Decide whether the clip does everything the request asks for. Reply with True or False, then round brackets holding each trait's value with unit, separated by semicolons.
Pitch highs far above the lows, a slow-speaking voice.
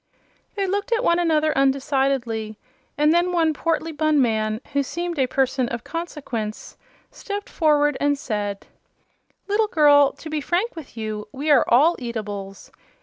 False (5.7 semitones; 150 wpm)